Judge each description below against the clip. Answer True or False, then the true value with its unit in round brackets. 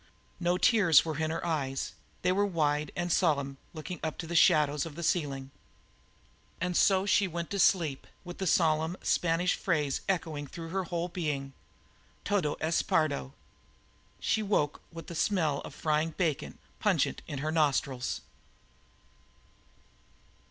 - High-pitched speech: False (165 Hz)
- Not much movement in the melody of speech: False (3.1 semitones)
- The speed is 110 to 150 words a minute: True (145 wpm)